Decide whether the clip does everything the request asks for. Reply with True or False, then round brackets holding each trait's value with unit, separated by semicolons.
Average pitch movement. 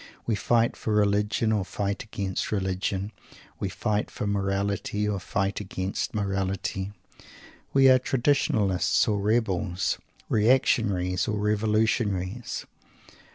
False (2.1 semitones)